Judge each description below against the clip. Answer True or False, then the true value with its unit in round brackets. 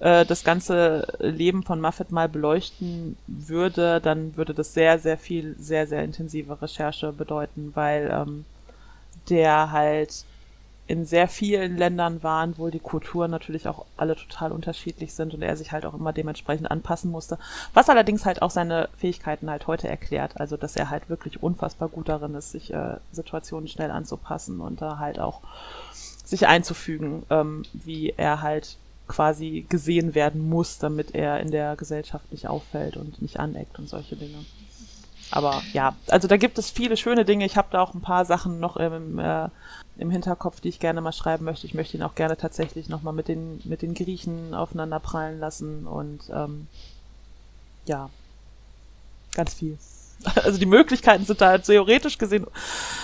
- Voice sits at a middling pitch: True (160 Hz)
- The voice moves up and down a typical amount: False (2.3 semitones)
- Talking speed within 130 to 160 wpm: False (170 wpm)